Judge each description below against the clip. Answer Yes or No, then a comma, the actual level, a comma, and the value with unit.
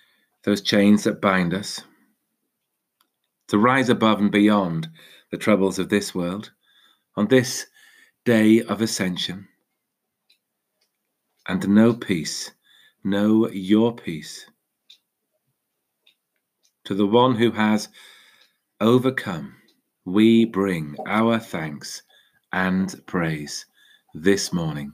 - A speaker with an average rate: No, slow, 100 wpm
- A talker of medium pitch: No, low, 105 Hz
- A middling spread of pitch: Yes, average, 3.0 semitones